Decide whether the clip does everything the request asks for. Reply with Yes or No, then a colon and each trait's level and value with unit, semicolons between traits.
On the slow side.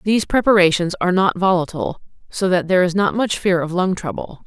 No: average, 200 wpm